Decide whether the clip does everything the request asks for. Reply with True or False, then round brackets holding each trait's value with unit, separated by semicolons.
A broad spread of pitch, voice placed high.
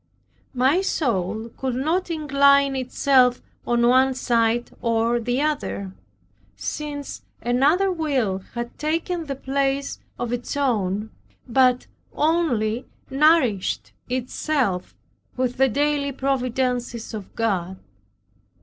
False (3.3 semitones; 255 Hz)